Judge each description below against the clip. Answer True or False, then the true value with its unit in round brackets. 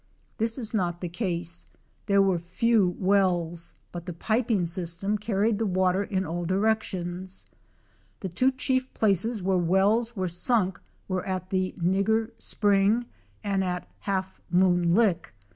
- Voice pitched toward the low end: False (190 Hz)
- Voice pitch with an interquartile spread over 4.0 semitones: False (3.3 semitones)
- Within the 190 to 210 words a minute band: False (145 wpm)